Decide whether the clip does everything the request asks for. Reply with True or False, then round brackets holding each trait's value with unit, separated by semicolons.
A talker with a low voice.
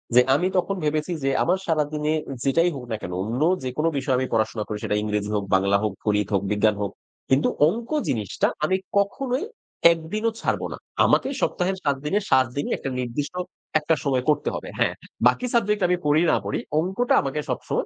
False (145 Hz)